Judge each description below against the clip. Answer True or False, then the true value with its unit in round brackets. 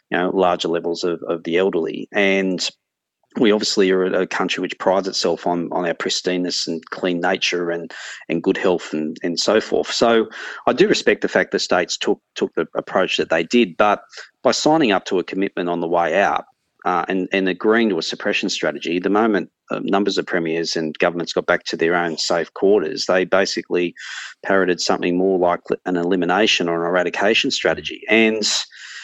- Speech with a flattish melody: True (2.2 semitones)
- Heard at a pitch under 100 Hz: True (90 Hz)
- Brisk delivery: False (195 wpm)